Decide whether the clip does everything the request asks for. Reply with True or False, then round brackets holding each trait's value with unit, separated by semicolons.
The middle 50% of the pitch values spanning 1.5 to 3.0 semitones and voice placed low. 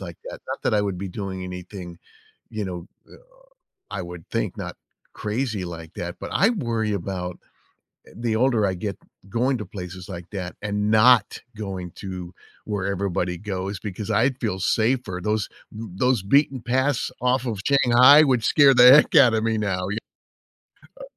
False (4.8 semitones; 105 Hz)